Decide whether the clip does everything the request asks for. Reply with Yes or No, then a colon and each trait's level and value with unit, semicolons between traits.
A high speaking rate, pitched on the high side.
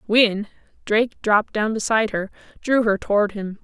No: average, 165 wpm; high, 215 Hz